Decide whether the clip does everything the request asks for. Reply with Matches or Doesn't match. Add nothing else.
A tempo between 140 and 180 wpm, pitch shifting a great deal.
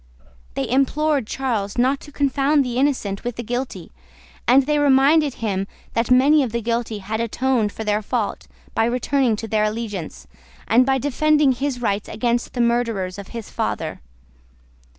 Doesn't match